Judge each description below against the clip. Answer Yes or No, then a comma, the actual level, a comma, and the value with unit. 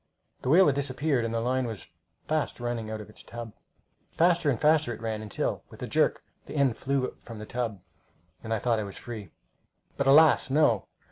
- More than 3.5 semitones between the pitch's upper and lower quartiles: Yes, average, 4.2 semitones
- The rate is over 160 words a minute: Yes, fast, 205 wpm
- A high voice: No, low, 120 Hz